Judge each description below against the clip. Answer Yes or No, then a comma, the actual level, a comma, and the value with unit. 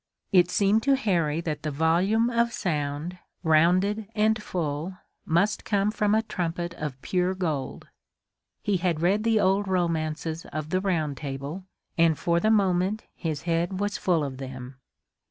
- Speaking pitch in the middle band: Yes, medium, 175 Hz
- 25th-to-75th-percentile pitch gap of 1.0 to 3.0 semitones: No, average, 4.3 semitones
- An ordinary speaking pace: Yes, average, 155 wpm